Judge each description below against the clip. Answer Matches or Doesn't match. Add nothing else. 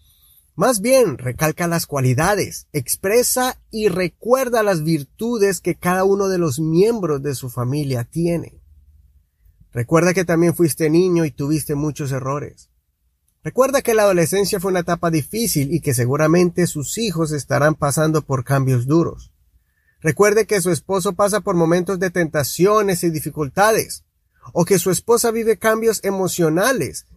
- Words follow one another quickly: Doesn't match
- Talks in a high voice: Doesn't match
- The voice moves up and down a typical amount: Doesn't match